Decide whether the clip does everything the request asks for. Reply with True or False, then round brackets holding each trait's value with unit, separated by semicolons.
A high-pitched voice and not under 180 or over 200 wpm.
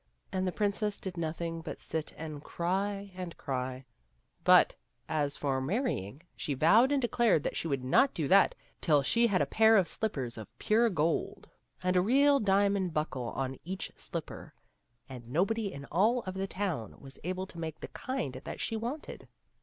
False (180 Hz; 185 wpm)